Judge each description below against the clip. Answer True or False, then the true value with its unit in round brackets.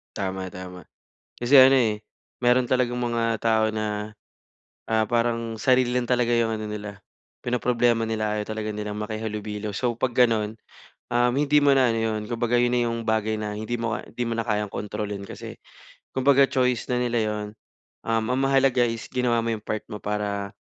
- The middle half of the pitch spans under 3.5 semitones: True (2.4 semitones)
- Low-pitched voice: True (115 Hz)